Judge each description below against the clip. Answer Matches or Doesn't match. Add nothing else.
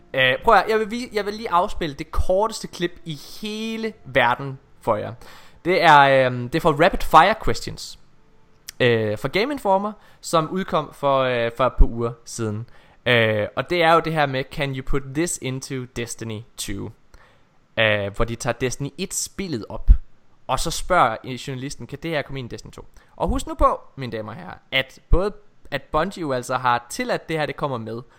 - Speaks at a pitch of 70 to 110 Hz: Doesn't match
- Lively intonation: Matches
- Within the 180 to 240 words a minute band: Matches